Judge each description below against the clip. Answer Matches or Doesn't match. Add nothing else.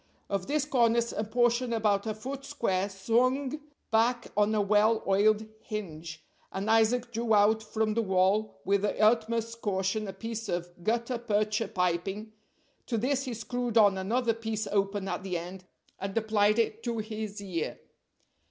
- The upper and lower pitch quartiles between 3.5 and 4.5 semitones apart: Doesn't match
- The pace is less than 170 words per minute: Matches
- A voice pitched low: Doesn't match